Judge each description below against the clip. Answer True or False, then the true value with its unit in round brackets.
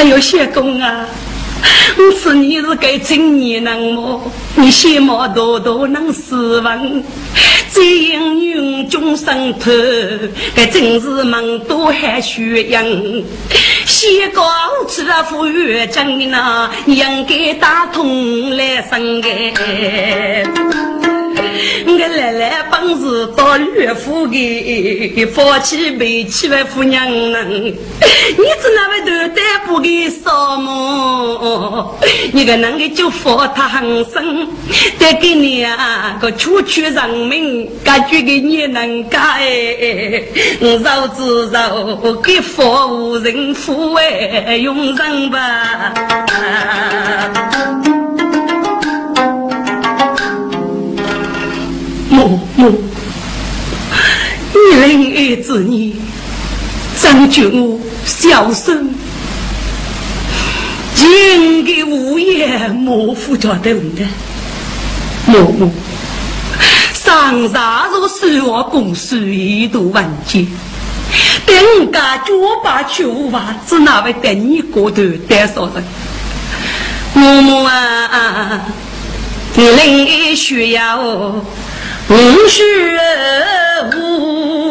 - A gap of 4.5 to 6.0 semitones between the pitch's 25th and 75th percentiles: True (5.3 semitones)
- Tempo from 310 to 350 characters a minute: False (115 characters per minute)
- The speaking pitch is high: True (265 Hz)